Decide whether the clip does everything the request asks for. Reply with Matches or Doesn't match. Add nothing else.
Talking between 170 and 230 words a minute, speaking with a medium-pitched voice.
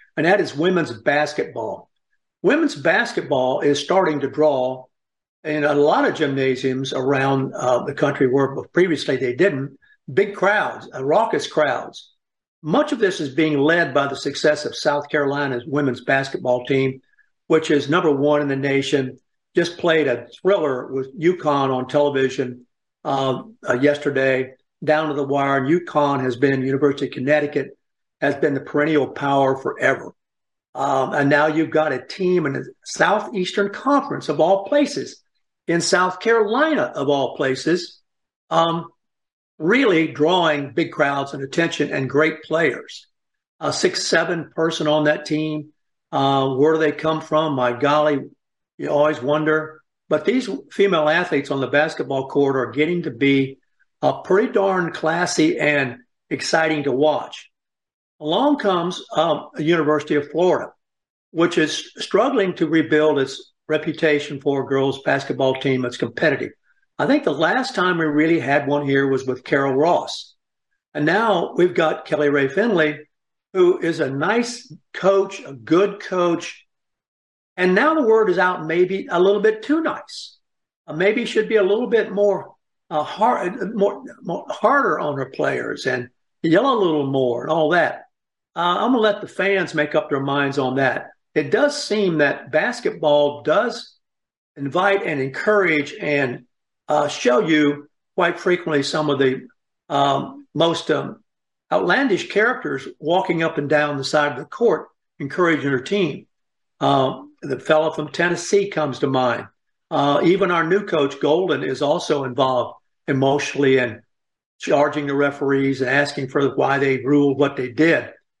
Doesn't match